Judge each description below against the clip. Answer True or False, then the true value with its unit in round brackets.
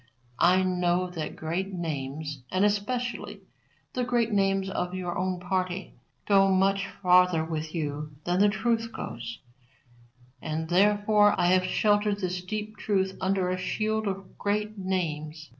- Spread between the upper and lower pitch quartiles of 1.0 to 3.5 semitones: True (2.8 semitones)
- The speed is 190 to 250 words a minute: False (140 wpm)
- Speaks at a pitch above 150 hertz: True (185 Hz)